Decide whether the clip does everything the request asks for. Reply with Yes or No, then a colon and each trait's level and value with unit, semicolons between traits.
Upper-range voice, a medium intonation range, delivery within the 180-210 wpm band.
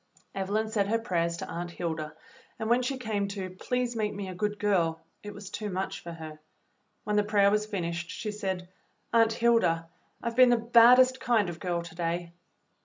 Yes: high, 205 Hz; average, 4.6 semitones; average, 195 wpm